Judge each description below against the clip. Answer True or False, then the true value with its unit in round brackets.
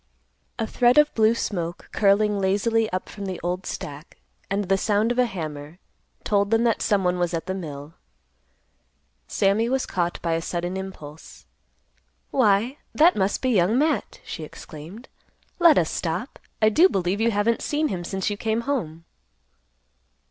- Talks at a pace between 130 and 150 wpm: False (165 wpm)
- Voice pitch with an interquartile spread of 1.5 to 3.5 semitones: False (4.5 semitones)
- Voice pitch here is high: True (200 Hz)